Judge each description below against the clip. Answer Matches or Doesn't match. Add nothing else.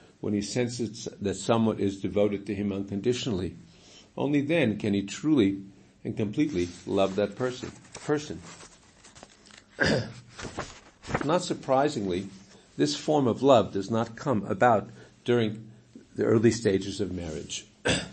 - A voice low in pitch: Matches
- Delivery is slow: Matches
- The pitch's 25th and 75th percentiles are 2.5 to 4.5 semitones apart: Matches